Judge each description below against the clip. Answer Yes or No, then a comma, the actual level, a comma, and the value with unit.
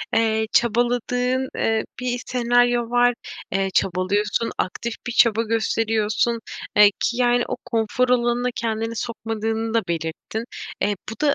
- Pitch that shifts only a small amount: Yes, narrow, 1.9 semitones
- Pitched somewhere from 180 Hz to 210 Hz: No, high, 230 Hz